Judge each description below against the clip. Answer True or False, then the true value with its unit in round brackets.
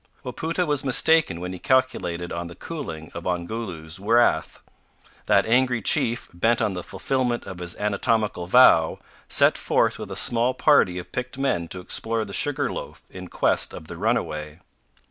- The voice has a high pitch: False (110 Hz)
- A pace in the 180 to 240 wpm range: False (165 wpm)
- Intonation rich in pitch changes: True (6.5 semitones)